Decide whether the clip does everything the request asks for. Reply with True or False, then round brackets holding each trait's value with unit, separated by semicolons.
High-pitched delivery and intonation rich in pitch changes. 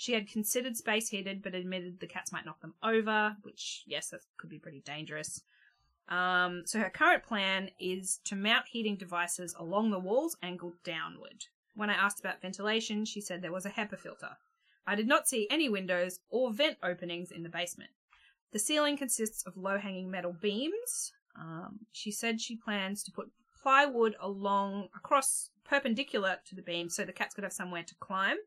False (200 Hz; 3.9 semitones)